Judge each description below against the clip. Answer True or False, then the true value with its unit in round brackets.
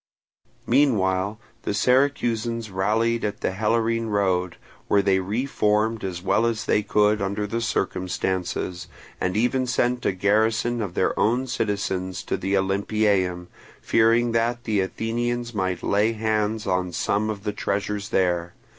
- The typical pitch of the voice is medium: False (105 Hz)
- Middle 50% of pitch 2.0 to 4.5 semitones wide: True (3.2 semitones)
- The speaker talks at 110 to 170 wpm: True (145 wpm)